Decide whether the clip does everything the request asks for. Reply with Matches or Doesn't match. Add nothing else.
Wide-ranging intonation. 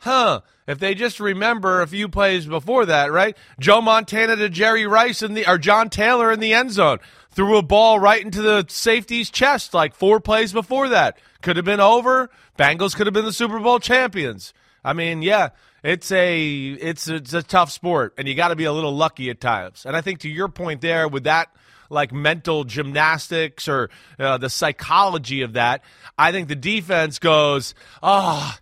Matches